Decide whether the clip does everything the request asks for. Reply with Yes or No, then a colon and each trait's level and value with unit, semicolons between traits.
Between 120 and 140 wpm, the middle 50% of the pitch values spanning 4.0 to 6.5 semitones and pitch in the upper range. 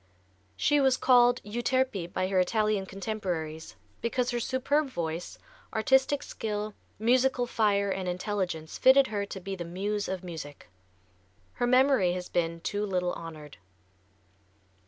Yes: slow, 135 wpm; wide, 5.4 semitones; high, 205 Hz